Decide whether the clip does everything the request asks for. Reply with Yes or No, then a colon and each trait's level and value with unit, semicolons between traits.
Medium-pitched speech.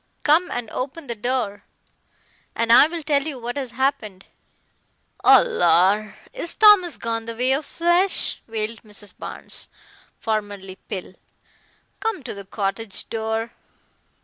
No: high, 230 Hz